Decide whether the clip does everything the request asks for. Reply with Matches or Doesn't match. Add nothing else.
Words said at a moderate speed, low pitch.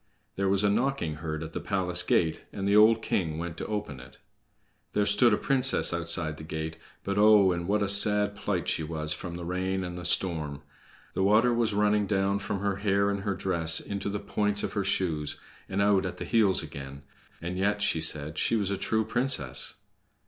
Doesn't match